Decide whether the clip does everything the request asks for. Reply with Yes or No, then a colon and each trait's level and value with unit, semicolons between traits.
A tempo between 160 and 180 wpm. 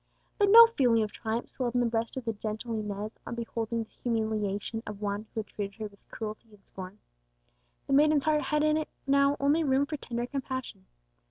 No: fast, 205 wpm